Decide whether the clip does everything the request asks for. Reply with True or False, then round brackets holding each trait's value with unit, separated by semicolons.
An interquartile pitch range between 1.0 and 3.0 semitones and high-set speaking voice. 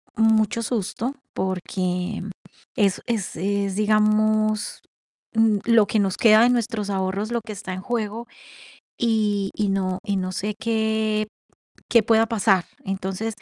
True (2.4 semitones; 215 Hz)